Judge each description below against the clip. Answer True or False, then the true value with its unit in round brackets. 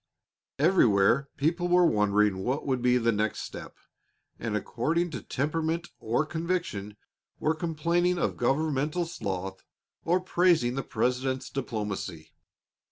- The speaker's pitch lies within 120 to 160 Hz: True (140 Hz)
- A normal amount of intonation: False (7.4 semitones)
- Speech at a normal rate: False (120 wpm)